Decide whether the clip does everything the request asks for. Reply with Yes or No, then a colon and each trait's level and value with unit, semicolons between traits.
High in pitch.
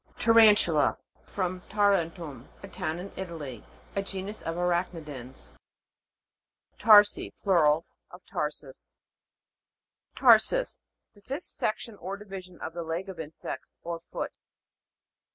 No: medium, 180 Hz